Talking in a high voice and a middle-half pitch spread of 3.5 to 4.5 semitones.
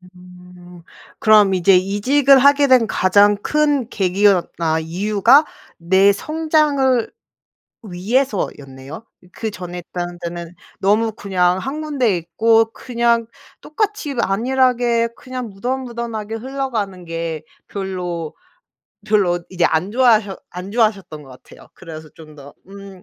No: high, 205 Hz; wide, 5.4 semitones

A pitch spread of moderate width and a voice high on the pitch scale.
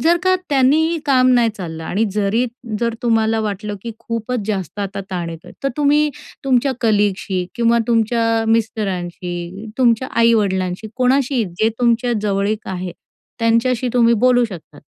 Yes: average, 3.8 semitones; high, 225 Hz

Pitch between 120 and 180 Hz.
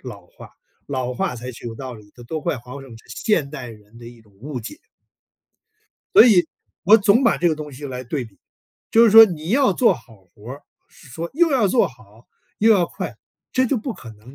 Yes: medium, 140 Hz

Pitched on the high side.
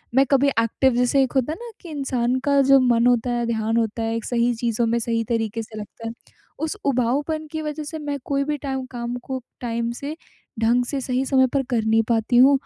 Yes: high, 245 Hz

